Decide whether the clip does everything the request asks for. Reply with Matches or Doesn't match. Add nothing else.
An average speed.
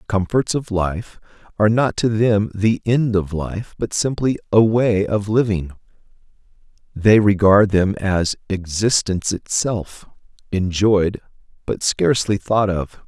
Doesn't match